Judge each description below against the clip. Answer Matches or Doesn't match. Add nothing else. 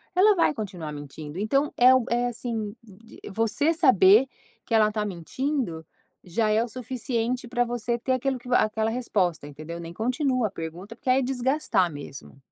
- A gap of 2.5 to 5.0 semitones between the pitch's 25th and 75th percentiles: Doesn't match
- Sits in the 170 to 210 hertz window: Doesn't match